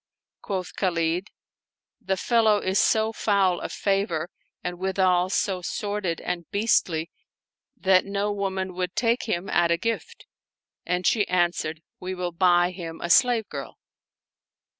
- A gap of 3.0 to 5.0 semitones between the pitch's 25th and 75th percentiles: No, narrow, 2.5 semitones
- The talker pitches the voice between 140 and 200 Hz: Yes, medium, 185 Hz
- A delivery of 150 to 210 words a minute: No, average, 140 wpm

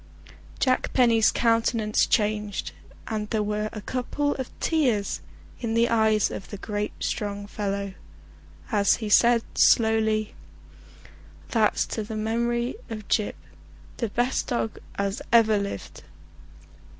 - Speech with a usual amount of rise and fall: No, narrow, 2.0 semitones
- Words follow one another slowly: Yes, slow, 125 wpm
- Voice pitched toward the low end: No, high, 220 Hz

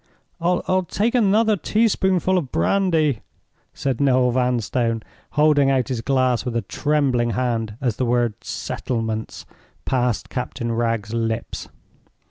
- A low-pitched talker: Yes, low, 125 Hz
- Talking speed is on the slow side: Yes, slow, 120 wpm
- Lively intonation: No, average, 4.9 semitones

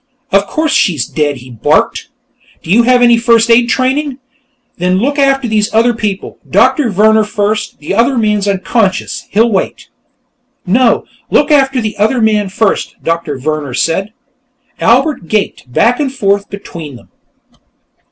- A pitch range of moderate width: Yes, average, 4.5 semitones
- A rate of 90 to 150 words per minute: Yes, average, 145 wpm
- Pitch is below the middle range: No, high, 215 Hz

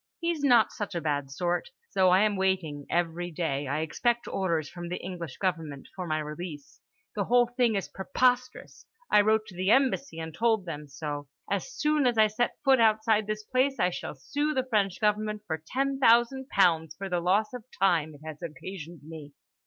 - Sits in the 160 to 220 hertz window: Yes, high, 190 Hz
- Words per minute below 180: No, average, 195 wpm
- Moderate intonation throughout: No, wide, 6.2 semitones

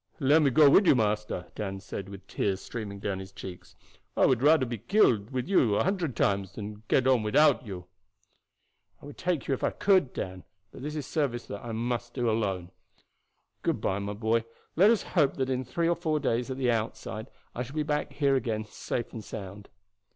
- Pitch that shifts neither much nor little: No, wide, 5.8 semitones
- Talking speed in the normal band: No, fast, 215 wpm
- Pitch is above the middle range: No, low, 120 Hz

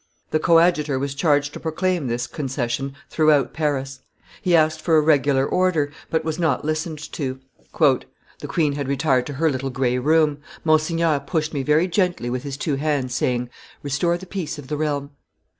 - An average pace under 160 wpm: No, average, 175 wpm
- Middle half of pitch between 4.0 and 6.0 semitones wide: No, average, 2.9 semitones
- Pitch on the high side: No, medium, 150 Hz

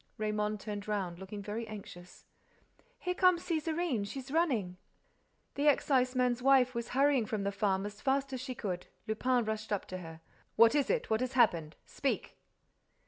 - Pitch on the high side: Yes, high, 230 Hz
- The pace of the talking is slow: No, average, 165 wpm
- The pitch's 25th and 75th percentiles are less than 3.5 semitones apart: No, average, 4.7 semitones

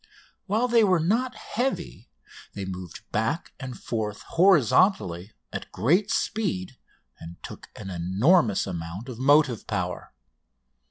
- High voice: No, low, 120 Hz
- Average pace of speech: No, slow, 120 wpm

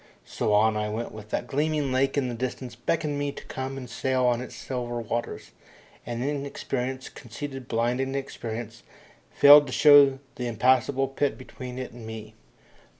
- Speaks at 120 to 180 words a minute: Yes, average, 165 wpm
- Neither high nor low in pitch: No, low, 130 Hz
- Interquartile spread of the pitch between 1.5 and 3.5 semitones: Yes, narrow, 2.4 semitones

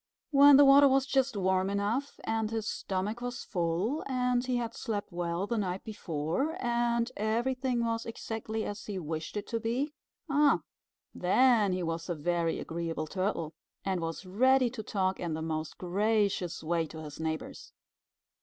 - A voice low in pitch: No, high, 210 Hz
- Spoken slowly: No, average, 165 wpm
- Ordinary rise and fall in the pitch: No, wide, 5.8 semitones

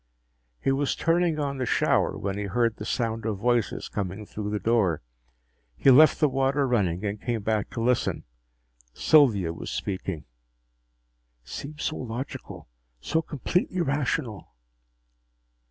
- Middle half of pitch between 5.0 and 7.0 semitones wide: Yes, wide, 5.6 semitones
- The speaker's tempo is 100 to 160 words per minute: Yes, average, 140 wpm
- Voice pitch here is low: Yes, low, 115 Hz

